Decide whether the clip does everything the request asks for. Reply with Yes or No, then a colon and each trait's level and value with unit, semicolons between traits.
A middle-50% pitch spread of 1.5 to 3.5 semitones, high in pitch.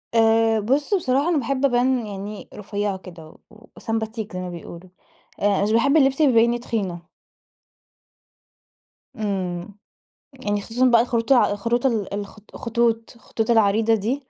Yes: average, 3.1 semitones; high, 225 Hz